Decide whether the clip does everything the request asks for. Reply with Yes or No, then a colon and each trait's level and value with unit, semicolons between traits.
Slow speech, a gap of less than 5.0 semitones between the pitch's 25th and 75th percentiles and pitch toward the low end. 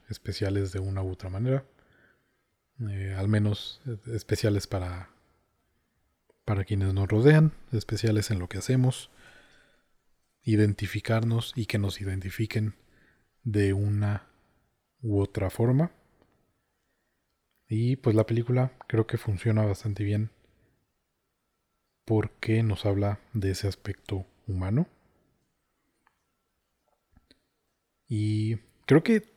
Yes: slow, 100 wpm; narrow, 2.5 semitones; low, 105 Hz